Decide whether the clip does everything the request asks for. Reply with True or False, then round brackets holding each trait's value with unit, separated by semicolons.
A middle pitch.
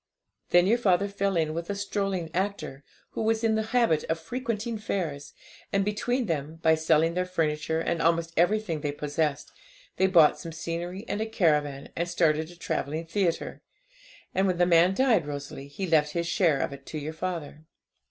True (170 Hz)